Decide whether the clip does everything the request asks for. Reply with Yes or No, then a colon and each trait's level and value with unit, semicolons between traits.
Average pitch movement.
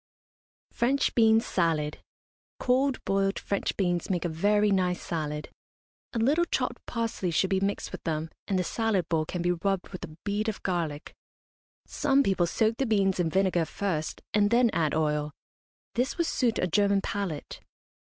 Yes: average, 4.7 semitones